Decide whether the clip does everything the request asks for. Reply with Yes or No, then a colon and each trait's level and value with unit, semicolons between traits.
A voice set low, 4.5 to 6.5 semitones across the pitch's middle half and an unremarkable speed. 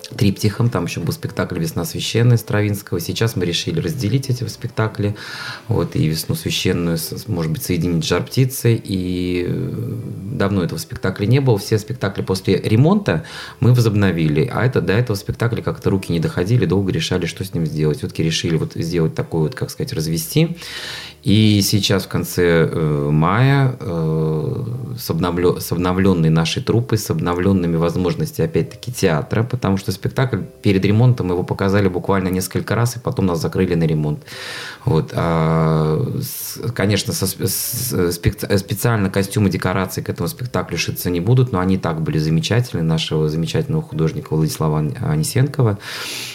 Yes: low, 100 Hz; average, 5.3 semitones; average, 150 wpm